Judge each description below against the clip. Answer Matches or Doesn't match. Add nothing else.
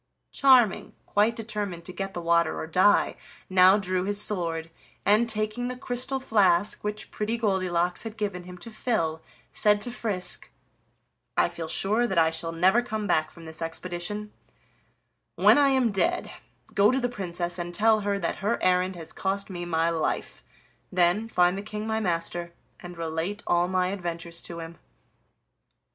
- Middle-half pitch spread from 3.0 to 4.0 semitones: Matches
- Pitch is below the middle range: Doesn't match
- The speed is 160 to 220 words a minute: Matches